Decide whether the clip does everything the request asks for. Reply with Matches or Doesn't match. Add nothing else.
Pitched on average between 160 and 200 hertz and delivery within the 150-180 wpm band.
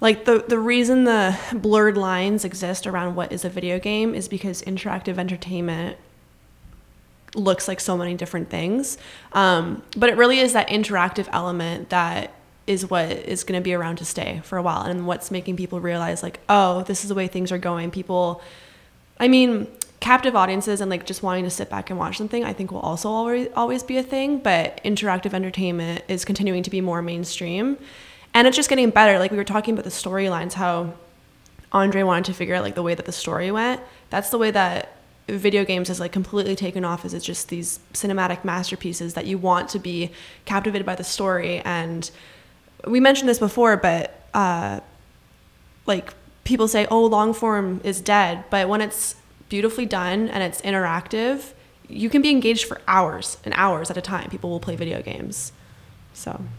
Doesn't match